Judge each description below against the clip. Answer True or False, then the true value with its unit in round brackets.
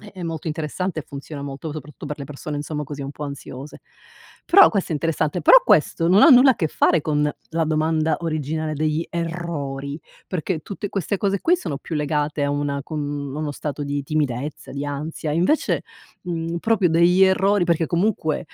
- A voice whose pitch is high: False (155 Hz)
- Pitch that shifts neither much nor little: True (3.0 semitones)